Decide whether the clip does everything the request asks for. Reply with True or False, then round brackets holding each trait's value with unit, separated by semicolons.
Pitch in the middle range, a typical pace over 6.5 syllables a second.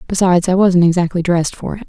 True (180 Hz; 7.0 syllables/s)